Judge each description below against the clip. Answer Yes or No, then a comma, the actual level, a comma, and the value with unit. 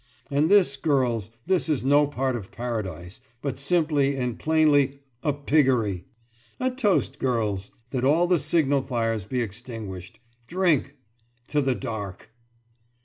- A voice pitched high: No, low, 135 Hz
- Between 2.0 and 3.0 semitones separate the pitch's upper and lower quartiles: No, average, 4.7 semitones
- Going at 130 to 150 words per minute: Yes, slow, 135 wpm